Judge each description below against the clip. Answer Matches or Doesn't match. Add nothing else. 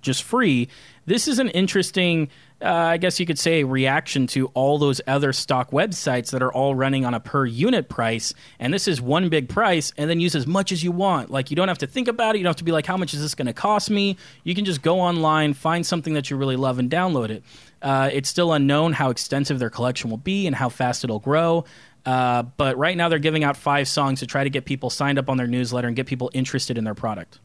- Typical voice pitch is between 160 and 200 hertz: Doesn't match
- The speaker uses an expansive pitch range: Doesn't match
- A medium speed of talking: Doesn't match